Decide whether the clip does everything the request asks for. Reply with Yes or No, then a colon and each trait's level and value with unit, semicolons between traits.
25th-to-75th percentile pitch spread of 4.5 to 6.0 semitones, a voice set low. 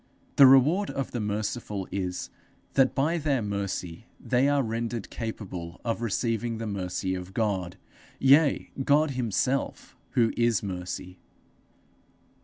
Yes: wide, 5.4 semitones; low, 115 Hz